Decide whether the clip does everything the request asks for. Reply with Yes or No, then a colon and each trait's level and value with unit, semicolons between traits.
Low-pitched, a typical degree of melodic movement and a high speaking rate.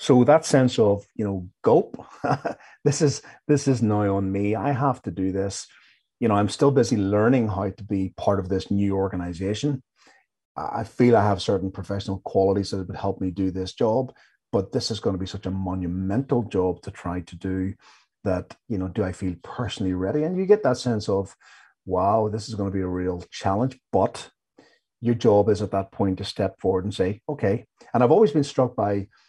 Yes: low, 100 Hz; average, 3.7 semitones; fast, 210 wpm